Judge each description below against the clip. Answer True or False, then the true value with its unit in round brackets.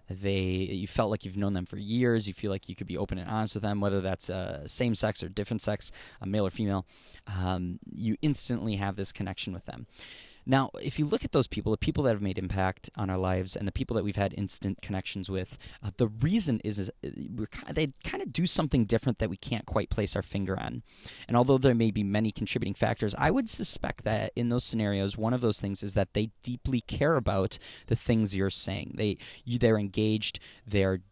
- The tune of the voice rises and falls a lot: False (3.3 semitones)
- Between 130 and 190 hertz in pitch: False (105 Hz)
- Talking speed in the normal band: False (230 wpm)